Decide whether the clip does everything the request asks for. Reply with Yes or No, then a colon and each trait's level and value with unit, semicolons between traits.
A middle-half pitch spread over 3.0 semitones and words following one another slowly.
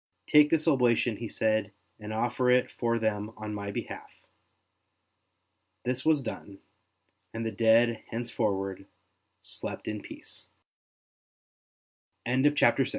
No: narrow, 2.5 semitones; slow, 115 wpm